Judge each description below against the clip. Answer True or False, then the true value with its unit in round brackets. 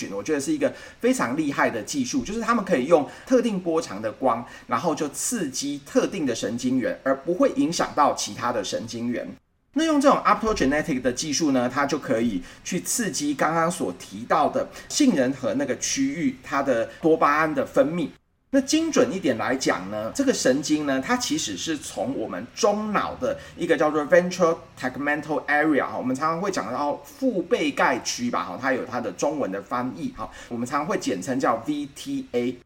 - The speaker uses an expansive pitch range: True (9.0 semitones)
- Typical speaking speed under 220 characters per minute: False (325 characters per minute)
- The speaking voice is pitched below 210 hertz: False (250 Hz)